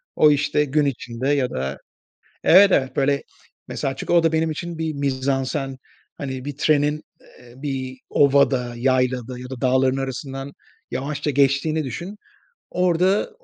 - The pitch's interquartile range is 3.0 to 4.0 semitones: No, narrow, 2.5 semitones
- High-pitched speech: No, medium, 140 Hz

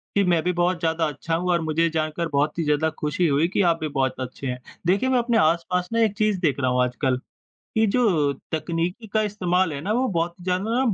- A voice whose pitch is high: No, medium, 170 Hz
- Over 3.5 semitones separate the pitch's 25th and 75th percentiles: Yes, average, 4.0 semitones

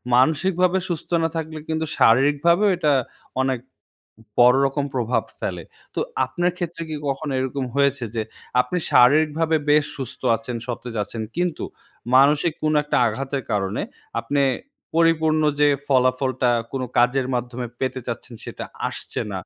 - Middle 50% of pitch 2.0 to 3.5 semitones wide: No, average, 4.0 semitones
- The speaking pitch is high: No, medium, 140 Hz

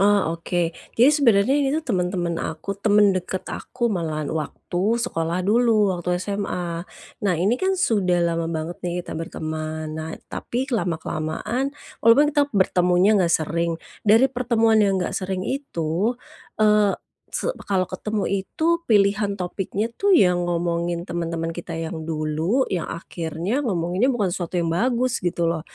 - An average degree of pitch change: Yes, average, 4.1 semitones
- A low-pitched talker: No, medium, 185 Hz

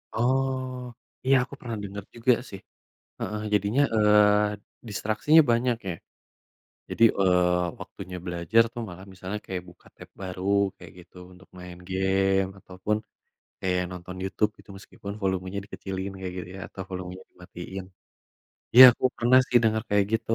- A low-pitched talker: Yes, very low, 95 Hz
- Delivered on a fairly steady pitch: No, average, 3.2 semitones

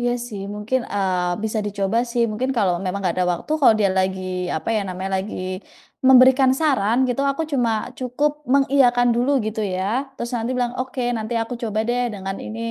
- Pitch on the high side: Yes, high, 230 Hz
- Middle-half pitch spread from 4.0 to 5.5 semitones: Yes, average, 4.5 semitones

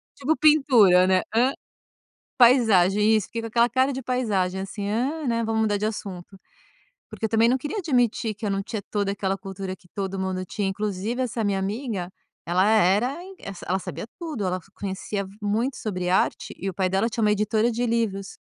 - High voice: Yes, high, 210 Hz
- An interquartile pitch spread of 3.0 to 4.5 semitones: Yes, average, 3.6 semitones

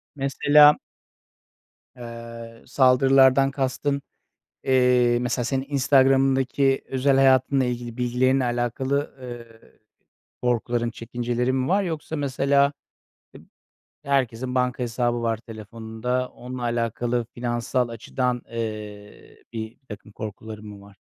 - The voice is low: Yes, low, 125 Hz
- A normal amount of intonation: No, narrow, 2.3 semitones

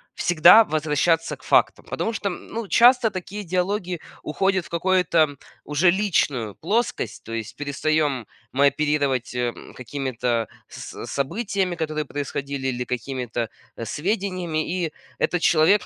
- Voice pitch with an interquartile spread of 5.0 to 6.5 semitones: Yes, average, 5.3 semitones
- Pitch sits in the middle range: Yes, medium, 155 Hz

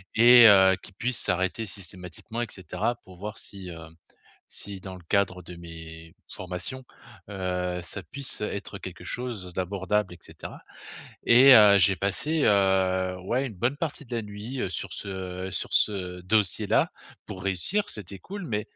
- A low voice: Yes, low, 100 Hz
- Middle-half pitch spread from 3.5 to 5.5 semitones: Yes, average, 3.9 semitones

